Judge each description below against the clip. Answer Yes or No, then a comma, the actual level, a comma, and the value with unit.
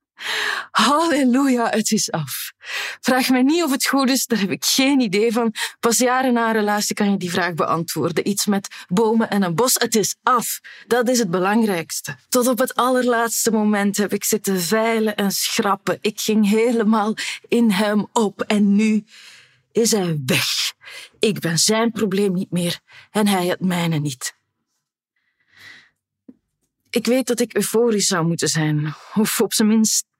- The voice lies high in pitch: Yes, high, 215 Hz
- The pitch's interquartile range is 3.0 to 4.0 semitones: Yes, average, 3.3 semitones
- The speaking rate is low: No, average, 170 wpm